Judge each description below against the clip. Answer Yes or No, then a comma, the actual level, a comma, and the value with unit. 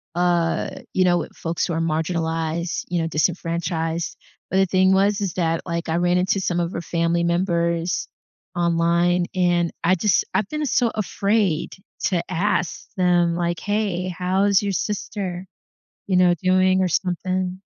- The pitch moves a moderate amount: No, narrow, 1.8 semitones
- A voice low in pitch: No, medium, 175 Hz